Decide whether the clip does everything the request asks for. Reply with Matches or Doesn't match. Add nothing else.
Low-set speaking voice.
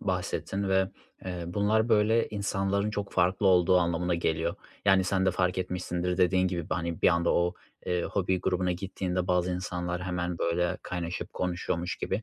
Matches